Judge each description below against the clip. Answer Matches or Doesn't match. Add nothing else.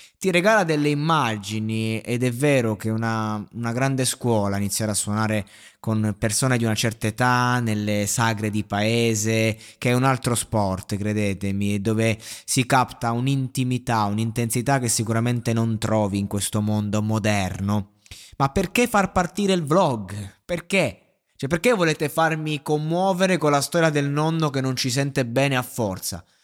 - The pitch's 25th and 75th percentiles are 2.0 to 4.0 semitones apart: Doesn't match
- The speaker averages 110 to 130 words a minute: Doesn't match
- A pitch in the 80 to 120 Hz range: Matches